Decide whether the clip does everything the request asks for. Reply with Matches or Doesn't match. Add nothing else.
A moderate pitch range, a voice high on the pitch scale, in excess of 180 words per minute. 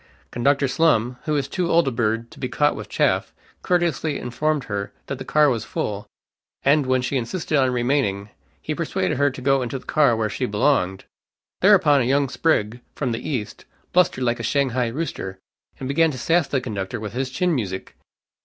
Doesn't match